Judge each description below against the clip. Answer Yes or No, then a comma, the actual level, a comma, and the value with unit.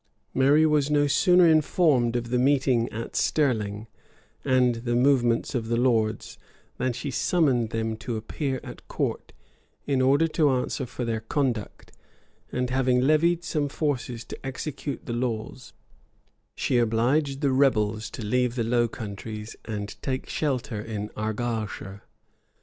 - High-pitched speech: No, low, 125 Hz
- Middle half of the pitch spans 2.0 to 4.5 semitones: Yes, average, 3.7 semitones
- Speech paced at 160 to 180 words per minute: No, average, 145 wpm